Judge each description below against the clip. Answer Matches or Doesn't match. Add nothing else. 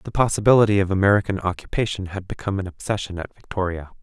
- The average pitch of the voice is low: Matches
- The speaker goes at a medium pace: Matches